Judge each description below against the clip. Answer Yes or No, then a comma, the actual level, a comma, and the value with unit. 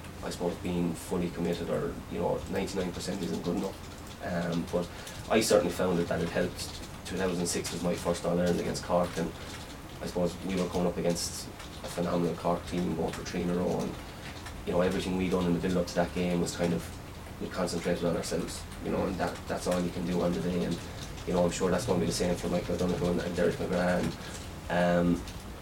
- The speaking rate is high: Yes, fast, 215 wpm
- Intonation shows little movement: Yes, narrow, 0.8 semitones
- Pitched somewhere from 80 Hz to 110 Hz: Yes, very low, 85 Hz